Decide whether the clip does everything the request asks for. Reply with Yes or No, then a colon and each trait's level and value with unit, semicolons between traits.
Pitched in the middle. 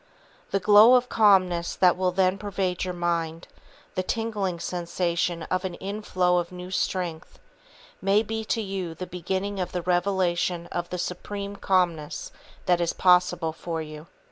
Yes: medium, 180 Hz